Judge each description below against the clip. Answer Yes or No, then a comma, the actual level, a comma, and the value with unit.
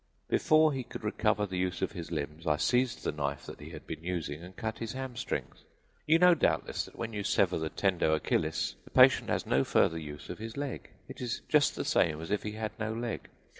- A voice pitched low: Yes, low, 100 Hz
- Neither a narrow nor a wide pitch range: No, wide, 6.7 semitones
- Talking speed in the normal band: No, fast, 230 wpm